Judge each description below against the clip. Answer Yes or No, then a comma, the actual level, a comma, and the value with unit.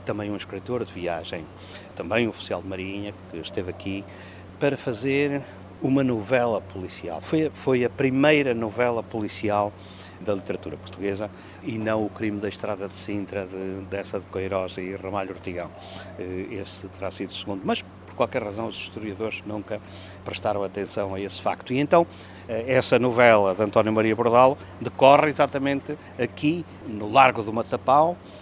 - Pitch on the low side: Yes, low, 100 Hz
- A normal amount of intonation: Yes, average, 4.1 semitones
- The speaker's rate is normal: Yes, average, 155 wpm